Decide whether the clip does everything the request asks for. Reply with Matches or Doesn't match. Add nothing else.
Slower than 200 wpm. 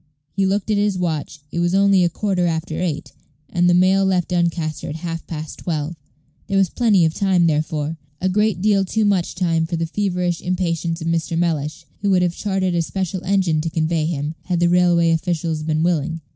Doesn't match